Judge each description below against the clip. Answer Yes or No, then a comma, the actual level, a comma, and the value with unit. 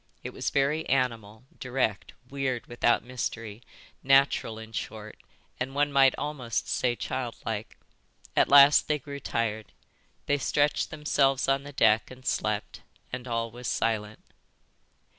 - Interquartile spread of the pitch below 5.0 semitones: Yes, average, 3.5 semitones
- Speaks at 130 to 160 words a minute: Yes, slow, 135 wpm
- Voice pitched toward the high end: No, low, 125 Hz